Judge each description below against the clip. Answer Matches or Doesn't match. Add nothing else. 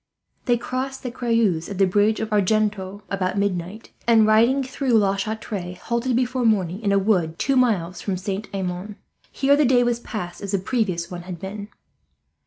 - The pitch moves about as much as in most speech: Matches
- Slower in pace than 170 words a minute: Doesn't match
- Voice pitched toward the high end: Matches